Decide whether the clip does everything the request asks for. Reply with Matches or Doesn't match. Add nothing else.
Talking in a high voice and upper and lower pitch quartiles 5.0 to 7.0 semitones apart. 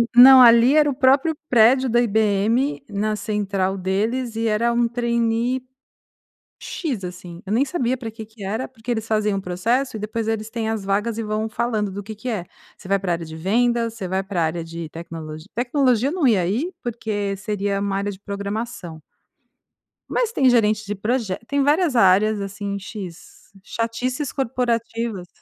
Doesn't match